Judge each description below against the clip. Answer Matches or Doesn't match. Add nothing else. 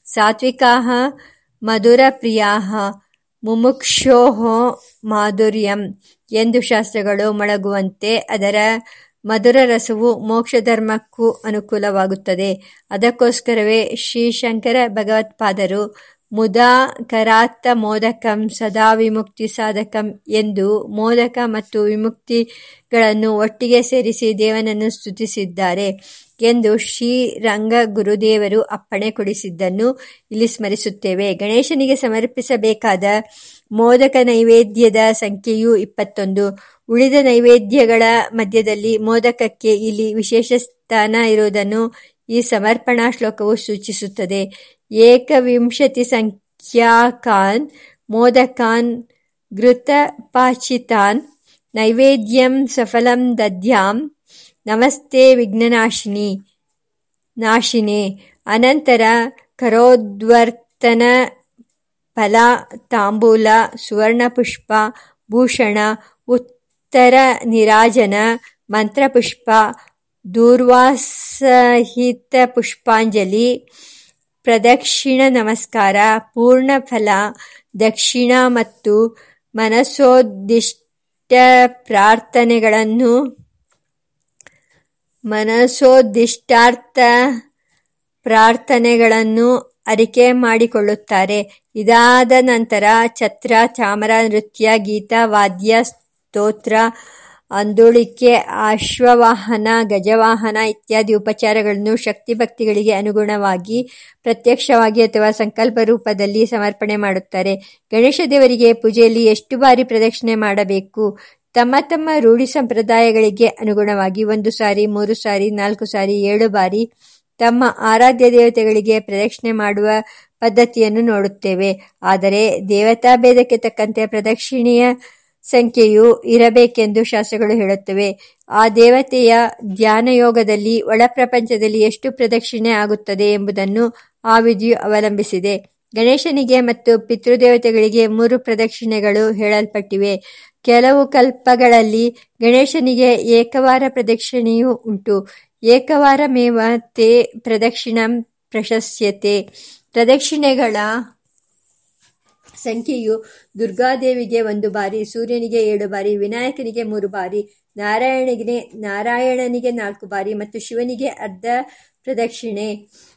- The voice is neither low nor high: Doesn't match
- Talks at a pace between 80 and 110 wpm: Doesn't match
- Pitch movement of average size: Doesn't match